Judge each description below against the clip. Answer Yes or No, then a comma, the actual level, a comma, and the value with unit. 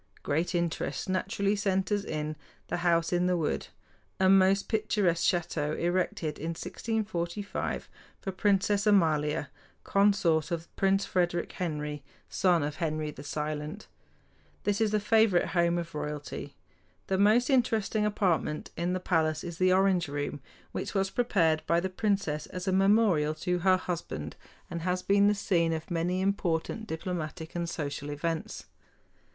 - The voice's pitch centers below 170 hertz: No, medium, 175 Hz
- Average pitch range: Yes, average, 3.7 semitones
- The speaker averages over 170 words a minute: No, average, 145 wpm